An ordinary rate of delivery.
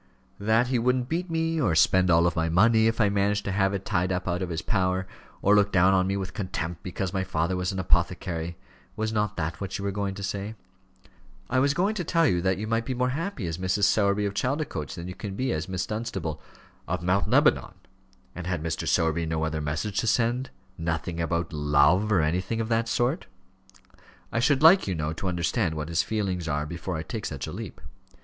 No: fast, 225 wpm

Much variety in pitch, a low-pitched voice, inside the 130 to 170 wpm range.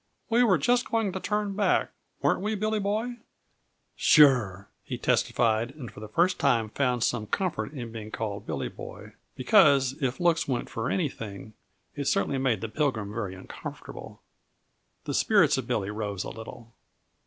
Yes: wide, 8.9 semitones; low, 130 Hz; average, 165 wpm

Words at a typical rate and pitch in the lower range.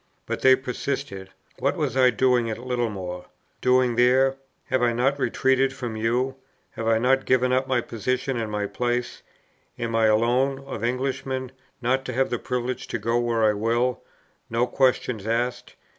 Yes: average, 170 wpm; low, 125 Hz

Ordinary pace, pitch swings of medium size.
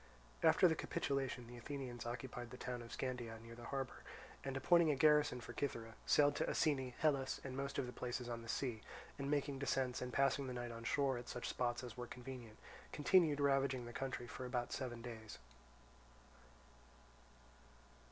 No: average, 180 wpm; narrow, 2.3 semitones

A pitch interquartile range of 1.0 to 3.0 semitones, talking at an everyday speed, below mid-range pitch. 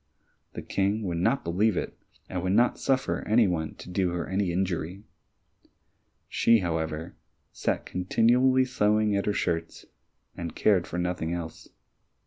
No: average, 3.8 semitones; average, 145 wpm; very low, 95 Hz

